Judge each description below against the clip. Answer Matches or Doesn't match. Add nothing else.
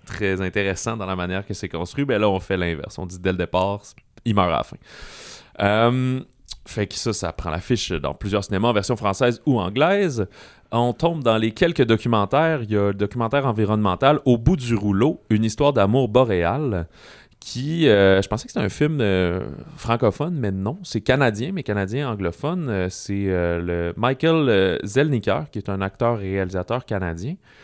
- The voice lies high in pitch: Doesn't match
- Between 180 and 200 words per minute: Matches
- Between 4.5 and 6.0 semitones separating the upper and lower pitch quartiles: Matches